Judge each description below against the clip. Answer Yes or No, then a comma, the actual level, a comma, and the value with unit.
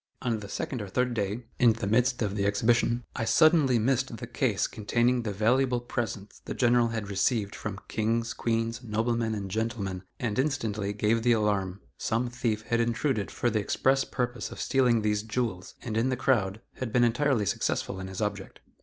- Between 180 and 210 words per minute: Yes, average, 190 wpm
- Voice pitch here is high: No, low, 115 Hz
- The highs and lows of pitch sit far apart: No, average, 2.8 semitones